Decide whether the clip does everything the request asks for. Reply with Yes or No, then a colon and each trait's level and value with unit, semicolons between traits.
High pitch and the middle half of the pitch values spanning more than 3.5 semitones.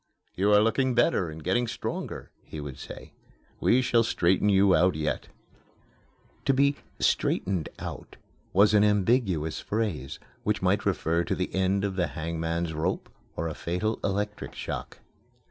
No: very low, 95 Hz; average, 4.4 semitones